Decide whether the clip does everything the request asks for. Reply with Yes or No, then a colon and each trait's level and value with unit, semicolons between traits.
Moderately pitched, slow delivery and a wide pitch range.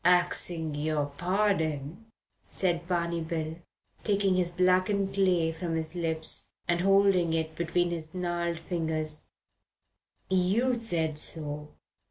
No: medium, 170 Hz; slow, 115 wpm; narrow, 2.4 semitones